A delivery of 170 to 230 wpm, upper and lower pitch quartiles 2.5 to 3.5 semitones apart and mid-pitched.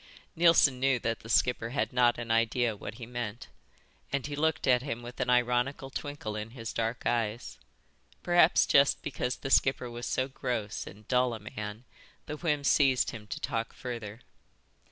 No: average, 175 wpm; average, 2.9 semitones; low, 125 Hz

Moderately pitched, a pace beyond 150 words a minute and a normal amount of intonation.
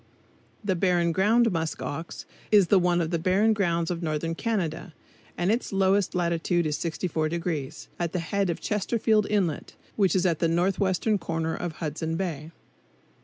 Yes: medium, 175 Hz; average, 165 wpm; average, 3.0 semitones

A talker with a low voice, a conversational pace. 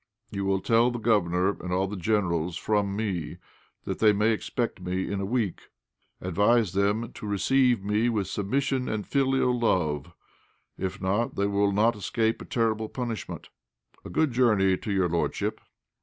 Yes: low, 105 Hz; average, 165 wpm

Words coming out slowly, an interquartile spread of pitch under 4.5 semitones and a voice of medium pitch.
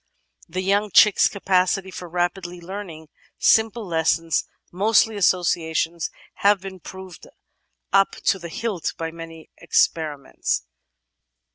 Yes: slow, 110 wpm; average, 3.1 semitones; medium, 180 Hz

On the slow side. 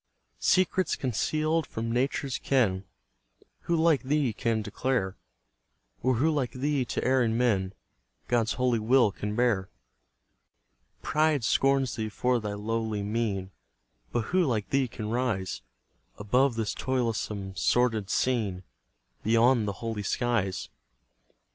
Yes: slow, 125 wpm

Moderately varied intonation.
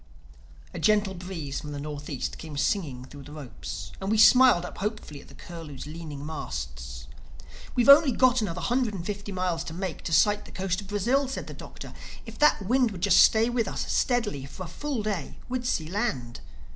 No: wide, 6.8 semitones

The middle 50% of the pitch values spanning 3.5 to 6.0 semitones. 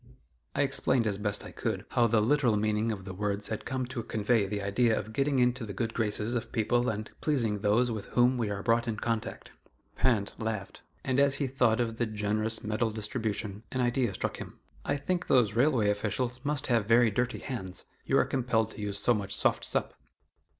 No: average, 2.9 semitones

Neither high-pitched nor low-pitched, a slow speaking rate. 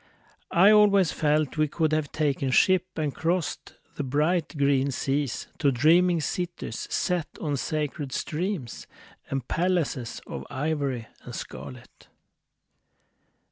Yes: medium, 150 Hz; slow, 120 wpm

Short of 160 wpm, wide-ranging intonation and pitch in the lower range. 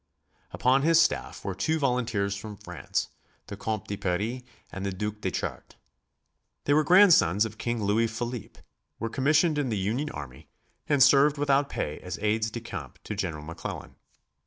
No: average, 170 wpm; wide, 5.8 semitones; low, 110 Hz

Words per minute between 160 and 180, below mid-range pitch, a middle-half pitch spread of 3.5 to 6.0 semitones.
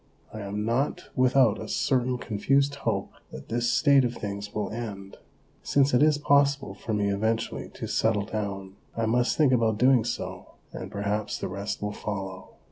Yes: average, 175 wpm; low, 110 Hz; average, 4.0 semitones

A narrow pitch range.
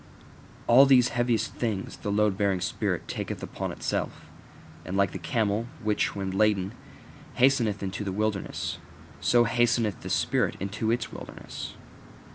No: average, 3.3 semitones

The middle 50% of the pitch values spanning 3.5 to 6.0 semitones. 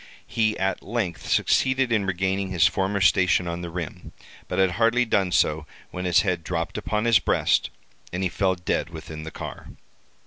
No: average, 2.9 semitones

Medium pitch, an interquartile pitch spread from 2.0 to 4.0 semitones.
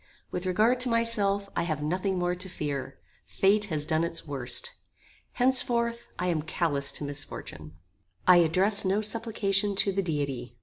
No: medium, 180 Hz; wide, 5.5 semitones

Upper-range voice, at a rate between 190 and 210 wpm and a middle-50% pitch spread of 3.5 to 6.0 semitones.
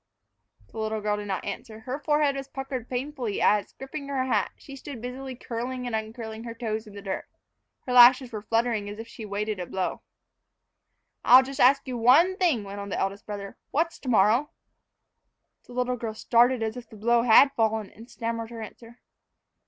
No: high, 235 Hz; average, 195 wpm; average, 3.1 semitones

